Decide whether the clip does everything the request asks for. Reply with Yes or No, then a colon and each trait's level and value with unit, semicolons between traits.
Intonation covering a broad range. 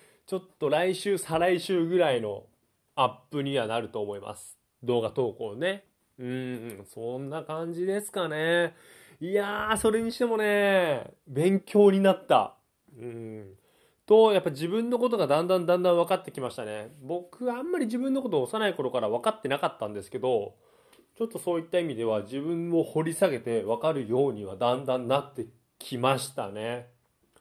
Yes: wide, 7.7 semitones